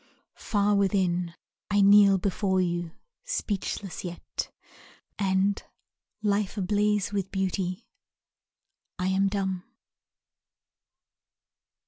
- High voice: Yes, high, 195 Hz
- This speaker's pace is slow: Yes, slow, 80 wpm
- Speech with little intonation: Yes, narrow, 1.7 semitones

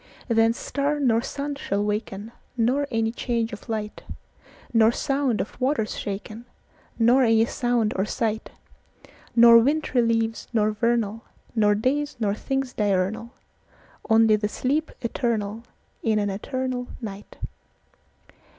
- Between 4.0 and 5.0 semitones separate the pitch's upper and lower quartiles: No, average, 3.0 semitones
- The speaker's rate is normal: No, slow, 105 wpm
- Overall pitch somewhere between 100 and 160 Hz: No, high, 230 Hz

